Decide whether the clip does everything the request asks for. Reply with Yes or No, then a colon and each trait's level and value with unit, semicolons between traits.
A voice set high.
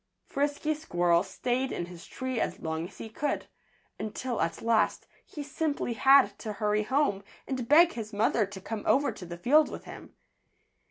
Yes: high, 230 Hz